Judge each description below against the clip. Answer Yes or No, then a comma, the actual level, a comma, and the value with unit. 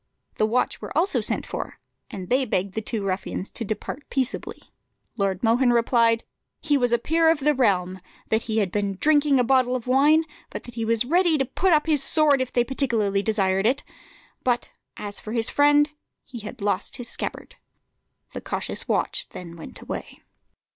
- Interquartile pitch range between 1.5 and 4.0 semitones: No, average, 4.9 semitones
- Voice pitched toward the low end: No, high, 240 Hz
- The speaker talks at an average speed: Yes, average, 190 wpm